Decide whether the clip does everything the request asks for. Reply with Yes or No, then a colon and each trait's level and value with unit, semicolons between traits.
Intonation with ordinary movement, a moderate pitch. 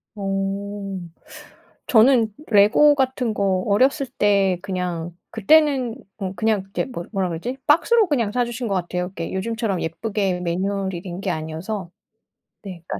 No: average, 4.0 semitones; high, 200 Hz